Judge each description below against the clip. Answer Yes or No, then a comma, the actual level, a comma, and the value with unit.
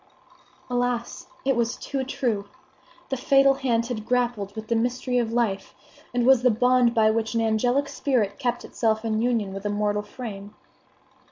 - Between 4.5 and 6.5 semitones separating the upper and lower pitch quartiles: No, narrow, 2.5 semitones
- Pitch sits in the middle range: No, high, 235 Hz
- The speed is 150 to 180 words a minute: Yes, average, 170 wpm